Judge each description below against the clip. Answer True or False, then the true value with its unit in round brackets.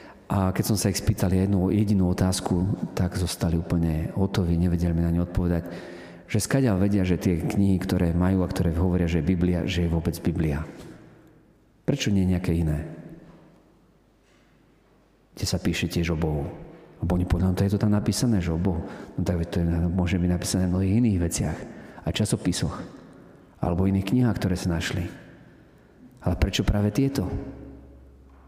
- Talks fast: True (170 wpm)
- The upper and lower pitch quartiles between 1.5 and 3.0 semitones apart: True (2.5 semitones)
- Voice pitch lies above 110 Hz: False (90 Hz)